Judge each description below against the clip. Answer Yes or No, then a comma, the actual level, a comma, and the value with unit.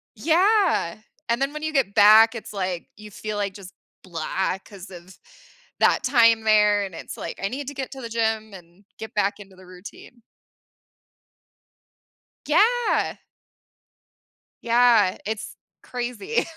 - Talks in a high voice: Yes, high, 220 Hz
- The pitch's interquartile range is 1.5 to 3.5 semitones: No, average, 4.3 semitones